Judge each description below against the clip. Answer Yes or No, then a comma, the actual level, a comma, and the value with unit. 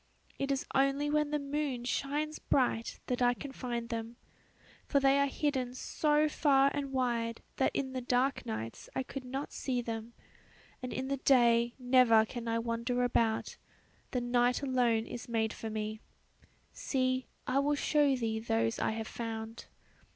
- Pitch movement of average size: Yes, average, 3.0 semitones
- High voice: Yes, very high, 250 Hz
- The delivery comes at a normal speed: Yes, average, 165 wpm